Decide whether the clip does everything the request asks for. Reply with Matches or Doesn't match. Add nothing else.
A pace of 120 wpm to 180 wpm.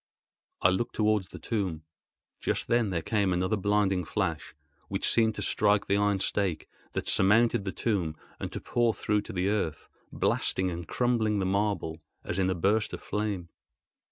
Matches